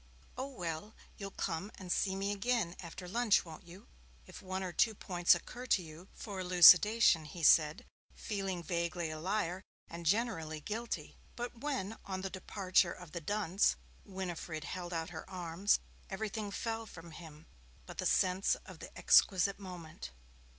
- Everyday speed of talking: Yes, average, 160 wpm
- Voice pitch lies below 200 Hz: Yes, medium, 185 Hz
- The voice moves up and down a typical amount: Yes, average, 3.2 semitones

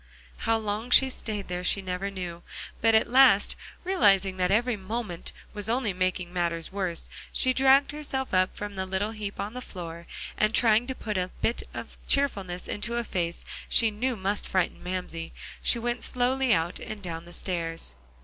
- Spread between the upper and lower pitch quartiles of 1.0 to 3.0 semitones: No, average, 4.5 semitones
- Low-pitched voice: No, high, 205 Hz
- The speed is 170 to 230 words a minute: Yes, average, 185 wpm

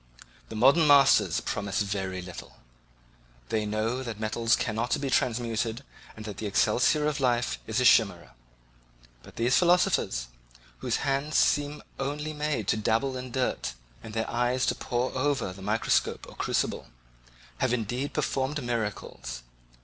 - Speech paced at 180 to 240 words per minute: No, average, 145 wpm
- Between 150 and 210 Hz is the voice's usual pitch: No, low, 120 Hz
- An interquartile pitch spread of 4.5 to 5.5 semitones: No, average, 4.0 semitones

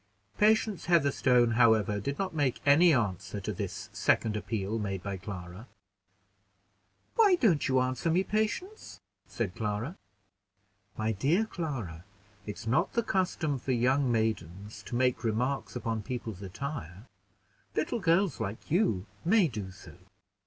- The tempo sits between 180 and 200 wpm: No, slow, 135 wpm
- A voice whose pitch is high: No, low, 125 Hz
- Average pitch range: No, wide, 8.0 semitones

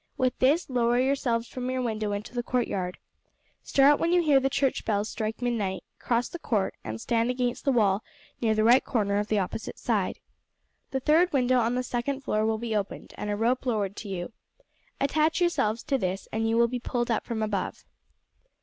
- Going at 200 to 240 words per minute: Yes, fast, 205 wpm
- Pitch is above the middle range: Yes, high, 235 Hz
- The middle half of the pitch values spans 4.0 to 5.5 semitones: No, average, 3.2 semitones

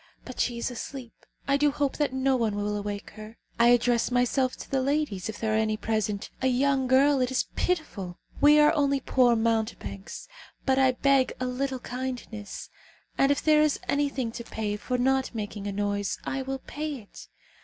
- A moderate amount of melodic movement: Yes, average, 3.9 semitones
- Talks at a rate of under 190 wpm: No, average, 195 wpm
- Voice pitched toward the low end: No, very high, 250 Hz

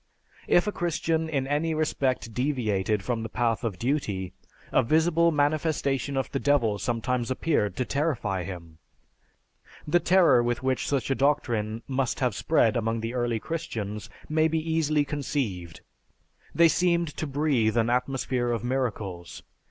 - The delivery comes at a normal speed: Yes, average, 145 wpm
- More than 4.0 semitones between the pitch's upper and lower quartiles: Yes, average, 5.2 semitones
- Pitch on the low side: Yes, low, 130 Hz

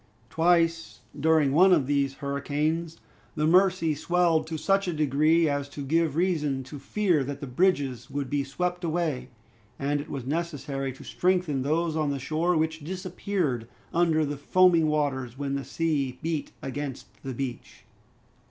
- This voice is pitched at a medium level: Yes, medium, 155 Hz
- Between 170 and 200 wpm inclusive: No, average, 160 wpm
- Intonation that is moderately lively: Yes, average, 3.3 semitones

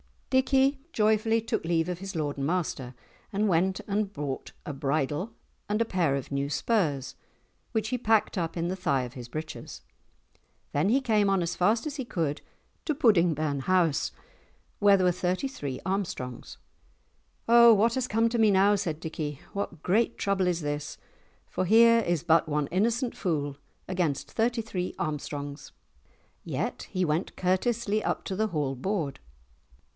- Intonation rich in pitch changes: Yes, wide, 6.3 semitones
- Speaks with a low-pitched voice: No, medium, 185 Hz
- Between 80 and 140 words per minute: No, average, 165 wpm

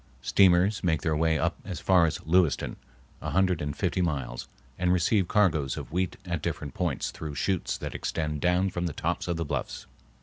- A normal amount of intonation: Yes, average, 3.0 semitones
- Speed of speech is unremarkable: Yes, average, 195 wpm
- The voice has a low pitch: Yes, very low, 85 Hz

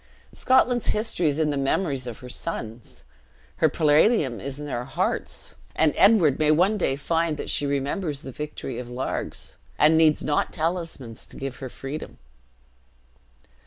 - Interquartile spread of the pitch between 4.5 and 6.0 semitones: No, average, 3.6 semitones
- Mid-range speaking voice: Yes, medium, 150 Hz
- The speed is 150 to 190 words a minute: Yes, average, 160 wpm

